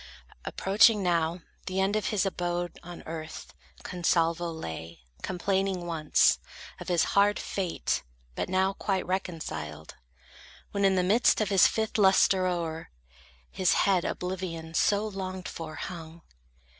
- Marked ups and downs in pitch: No, average, 2.8 semitones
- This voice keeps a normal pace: No, slow, 130 wpm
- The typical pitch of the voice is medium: Yes, medium, 180 Hz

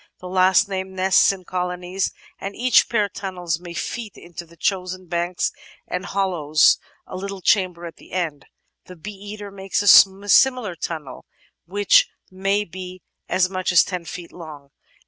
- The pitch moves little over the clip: Yes, narrow, 2.1 semitones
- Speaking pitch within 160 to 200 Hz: Yes, medium, 185 Hz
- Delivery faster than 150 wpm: Yes, average, 160 wpm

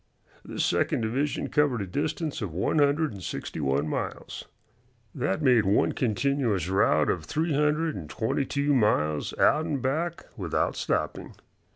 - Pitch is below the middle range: Yes, low, 130 Hz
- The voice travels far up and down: Yes, wide, 7.5 semitones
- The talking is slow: No, average, 155 wpm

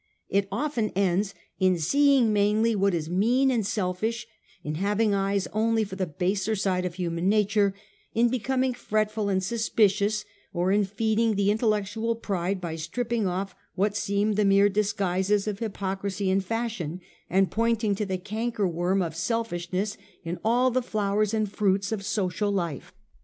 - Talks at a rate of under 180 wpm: Yes, average, 155 wpm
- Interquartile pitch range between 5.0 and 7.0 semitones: No, average, 2.7 semitones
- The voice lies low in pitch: No, high, 200 Hz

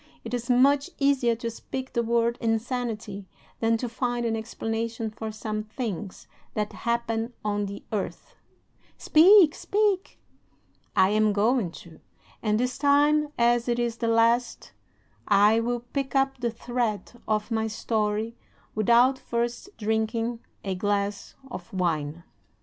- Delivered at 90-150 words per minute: Yes, average, 140 wpm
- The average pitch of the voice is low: No, high, 230 Hz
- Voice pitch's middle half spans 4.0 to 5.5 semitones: No, narrow, 2.4 semitones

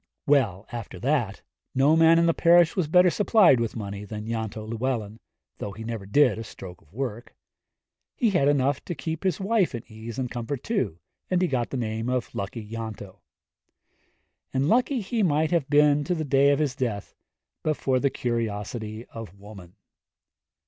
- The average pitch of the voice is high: No, low, 125 Hz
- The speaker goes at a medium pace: Yes, average, 180 wpm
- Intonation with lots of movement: Yes, wide, 6.0 semitones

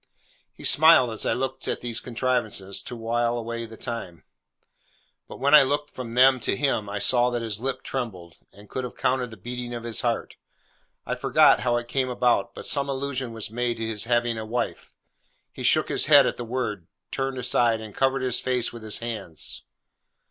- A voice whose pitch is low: Yes, low, 120 Hz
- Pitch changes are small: Yes, narrow, 2.3 semitones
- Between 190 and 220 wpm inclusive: Yes, average, 200 wpm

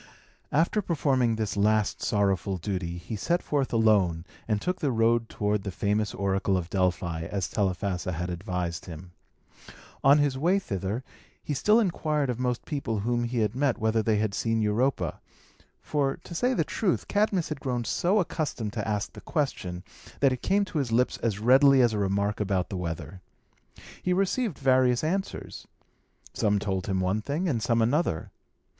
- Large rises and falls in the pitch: Yes, wide, 6.2 semitones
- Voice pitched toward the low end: Yes, low, 115 Hz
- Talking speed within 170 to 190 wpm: Yes, average, 175 wpm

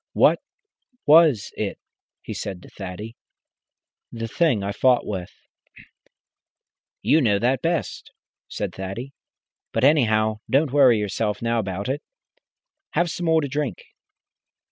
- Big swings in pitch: Yes, wide, 5.9 semitones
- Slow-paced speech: Yes, slow, 125 wpm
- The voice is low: Yes, low, 115 Hz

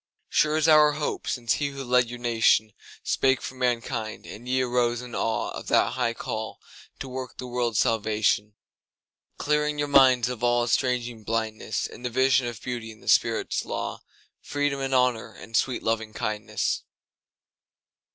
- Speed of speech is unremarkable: Yes, average, 145 wpm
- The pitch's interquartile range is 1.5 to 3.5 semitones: Yes, narrow, 2.6 semitones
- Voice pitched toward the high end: No, low, 120 Hz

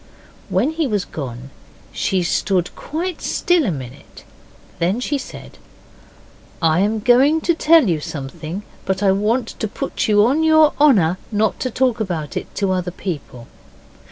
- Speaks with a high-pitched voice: Yes, high, 205 Hz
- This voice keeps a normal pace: Yes, average, 155 wpm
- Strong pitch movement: Yes, wide, 7.6 semitones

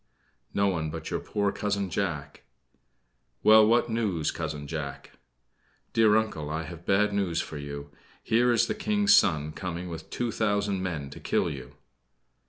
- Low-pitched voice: Yes, very low, 95 Hz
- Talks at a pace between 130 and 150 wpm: No, average, 160 wpm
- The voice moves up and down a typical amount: No, wide, 5.8 semitones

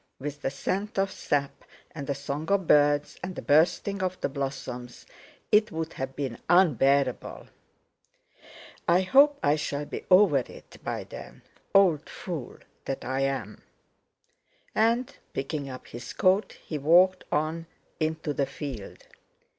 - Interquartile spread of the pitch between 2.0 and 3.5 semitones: No, average, 5.1 semitones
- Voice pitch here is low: No, medium, 150 Hz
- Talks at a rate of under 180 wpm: Yes, average, 140 wpm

